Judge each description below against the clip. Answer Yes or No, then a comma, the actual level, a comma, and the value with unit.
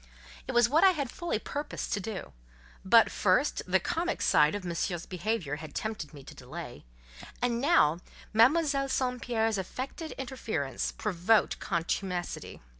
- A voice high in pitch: Yes, high, 220 Hz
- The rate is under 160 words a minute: Yes, average, 145 wpm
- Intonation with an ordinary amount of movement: No, wide, 7.1 semitones